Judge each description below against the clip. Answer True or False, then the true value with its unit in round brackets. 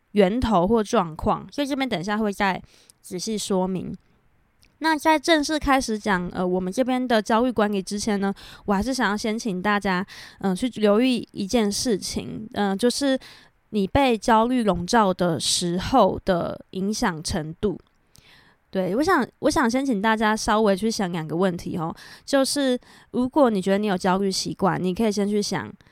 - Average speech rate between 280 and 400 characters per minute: False (255 characters per minute)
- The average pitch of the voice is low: False (210 Hz)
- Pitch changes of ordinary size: True (4.2 semitones)